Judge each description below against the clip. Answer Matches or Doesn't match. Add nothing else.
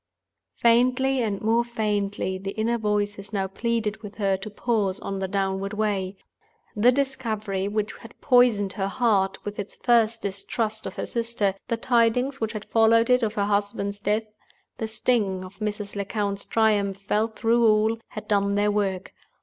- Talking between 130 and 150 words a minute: Doesn't match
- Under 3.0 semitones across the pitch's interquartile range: Matches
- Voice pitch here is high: Matches